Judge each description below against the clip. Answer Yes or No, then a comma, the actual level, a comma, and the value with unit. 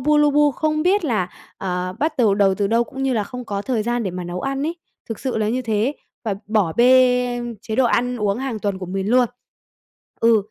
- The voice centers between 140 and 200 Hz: No, high, 235 Hz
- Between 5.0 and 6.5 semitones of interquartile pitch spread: No, average, 4.4 semitones